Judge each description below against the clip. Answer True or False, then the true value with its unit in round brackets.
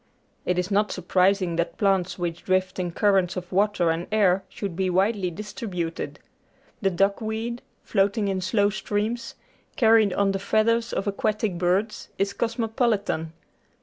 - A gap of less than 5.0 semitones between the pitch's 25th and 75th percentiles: True (2.8 semitones)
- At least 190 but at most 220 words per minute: False (150 wpm)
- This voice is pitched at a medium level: False (195 Hz)